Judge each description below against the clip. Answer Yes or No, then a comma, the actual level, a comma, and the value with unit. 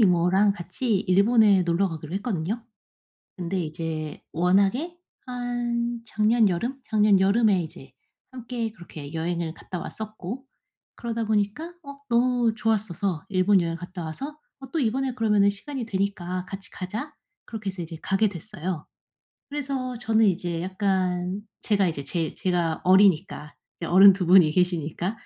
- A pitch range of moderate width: Yes, average, 4.5 semitones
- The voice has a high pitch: Yes, high, 195 Hz